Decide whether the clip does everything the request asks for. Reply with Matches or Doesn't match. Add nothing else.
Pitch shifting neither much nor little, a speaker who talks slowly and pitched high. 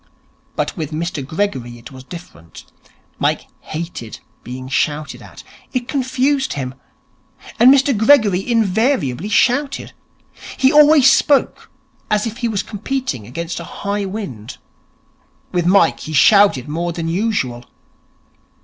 Doesn't match